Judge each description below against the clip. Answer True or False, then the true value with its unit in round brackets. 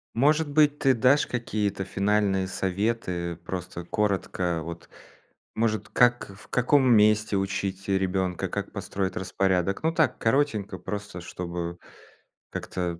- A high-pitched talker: False (100 Hz)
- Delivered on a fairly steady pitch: False (3.9 semitones)